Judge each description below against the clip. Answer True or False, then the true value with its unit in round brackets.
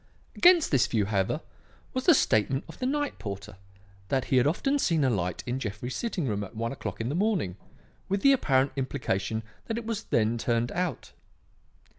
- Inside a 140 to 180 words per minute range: False (190 wpm)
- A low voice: True (130 Hz)